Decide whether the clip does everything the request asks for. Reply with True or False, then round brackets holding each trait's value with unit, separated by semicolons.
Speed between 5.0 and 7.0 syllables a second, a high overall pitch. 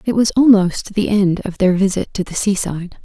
True (5.2 syllables/s; 195 Hz)